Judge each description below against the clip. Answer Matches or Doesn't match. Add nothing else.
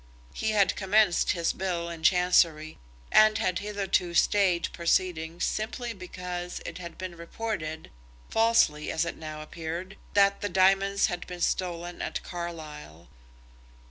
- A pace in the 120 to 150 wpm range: Matches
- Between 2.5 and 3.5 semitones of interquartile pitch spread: Matches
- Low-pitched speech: Doesn't match